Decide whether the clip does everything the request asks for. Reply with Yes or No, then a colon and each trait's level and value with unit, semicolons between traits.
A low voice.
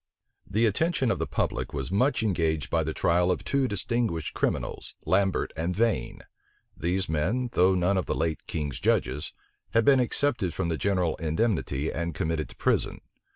Yes: very low, 90 Hz